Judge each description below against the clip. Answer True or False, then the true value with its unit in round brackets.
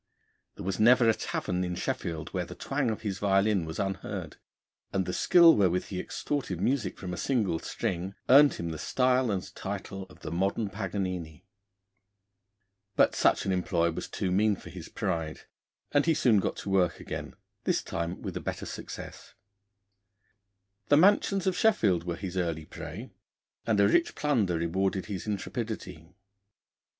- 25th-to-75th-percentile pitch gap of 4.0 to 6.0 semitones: True (4.6 semitones)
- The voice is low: True (95 Hz)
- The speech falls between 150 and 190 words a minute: True (165 wpm)